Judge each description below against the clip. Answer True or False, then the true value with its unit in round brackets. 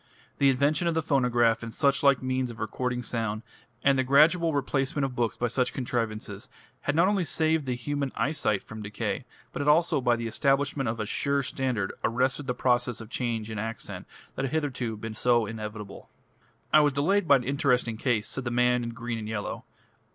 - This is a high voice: False (125 Hz)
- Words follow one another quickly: False (195 wpm)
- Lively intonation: False (3.6 semitones)